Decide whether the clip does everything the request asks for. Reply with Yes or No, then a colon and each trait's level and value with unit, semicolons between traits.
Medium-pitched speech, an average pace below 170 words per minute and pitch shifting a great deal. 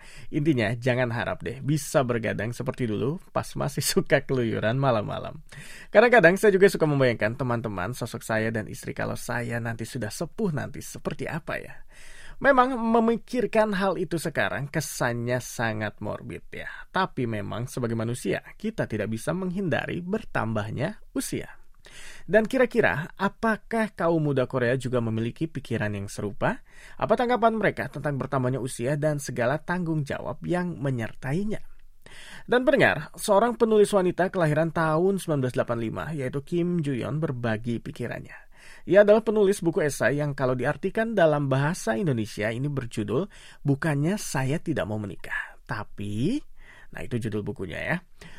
Yes: medium, 145 Hz; fast, 140 wpm; wide, 7.4 semitones